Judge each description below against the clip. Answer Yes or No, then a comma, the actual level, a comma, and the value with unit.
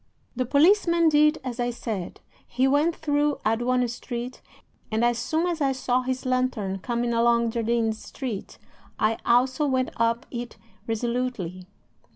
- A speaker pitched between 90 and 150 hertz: No, high, 245 Hz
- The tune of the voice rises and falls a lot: No, narrow, 2.5 semitones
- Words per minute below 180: Yes, average, 145 wpm